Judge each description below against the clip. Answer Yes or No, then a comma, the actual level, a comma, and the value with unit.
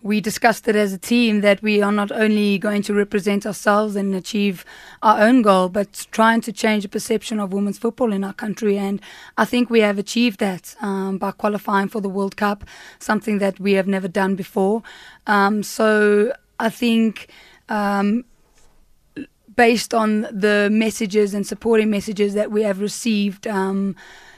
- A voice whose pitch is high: Yes, high, 210 Hz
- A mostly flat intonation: Yes, narrow, 1.7 semitones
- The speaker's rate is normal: Yes, average, 170 wpm